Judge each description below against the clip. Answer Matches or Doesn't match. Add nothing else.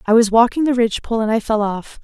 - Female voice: Matches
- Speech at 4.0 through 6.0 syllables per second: Doesn't match